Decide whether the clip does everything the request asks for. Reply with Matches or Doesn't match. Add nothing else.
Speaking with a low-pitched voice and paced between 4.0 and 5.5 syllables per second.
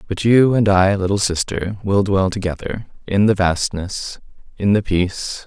Matches